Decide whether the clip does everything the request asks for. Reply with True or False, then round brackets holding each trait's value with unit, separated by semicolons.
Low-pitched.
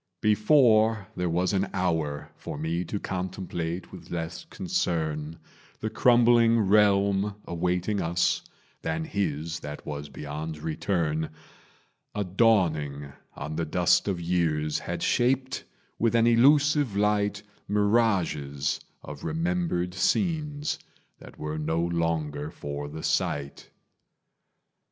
True (90 Hz)